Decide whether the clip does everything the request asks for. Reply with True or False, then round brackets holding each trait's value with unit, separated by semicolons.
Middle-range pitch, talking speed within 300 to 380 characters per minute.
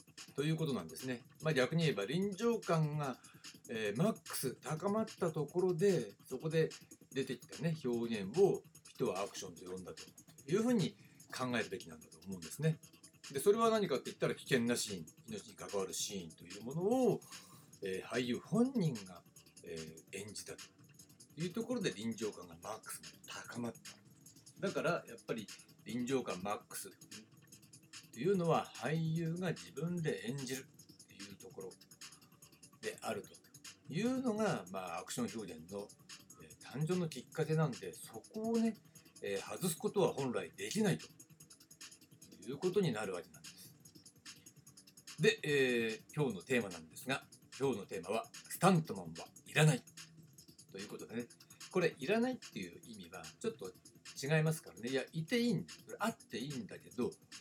True (160 Hz; 325 characters per minute)